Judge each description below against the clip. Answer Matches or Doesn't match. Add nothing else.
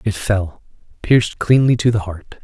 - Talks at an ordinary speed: Matches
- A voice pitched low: Matches